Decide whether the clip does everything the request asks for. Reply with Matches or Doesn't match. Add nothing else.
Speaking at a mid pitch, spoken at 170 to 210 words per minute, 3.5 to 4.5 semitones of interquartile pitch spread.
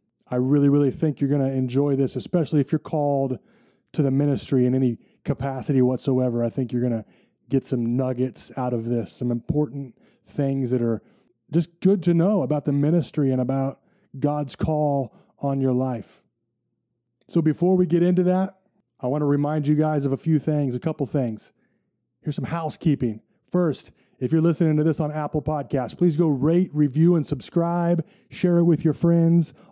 Matches